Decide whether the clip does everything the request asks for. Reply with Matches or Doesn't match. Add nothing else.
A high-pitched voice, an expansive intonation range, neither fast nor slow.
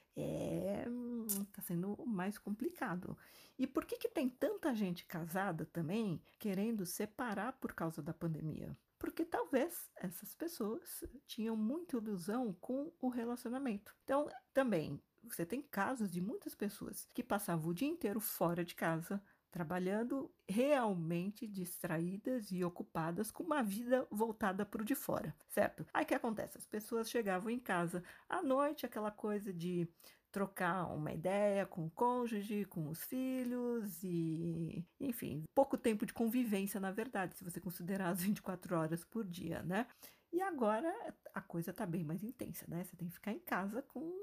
Matches